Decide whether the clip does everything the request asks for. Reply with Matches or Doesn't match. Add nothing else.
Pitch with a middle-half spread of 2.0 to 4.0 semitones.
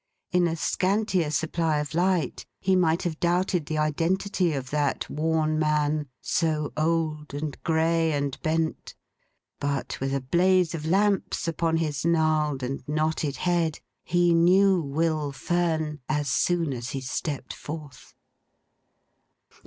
Matches